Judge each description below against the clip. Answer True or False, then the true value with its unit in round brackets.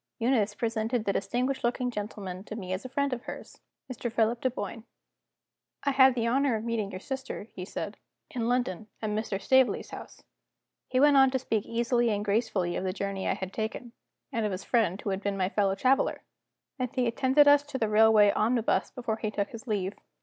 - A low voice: False (225 Hz)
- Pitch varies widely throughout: False (3.7 semitones)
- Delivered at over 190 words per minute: True (205 wpm)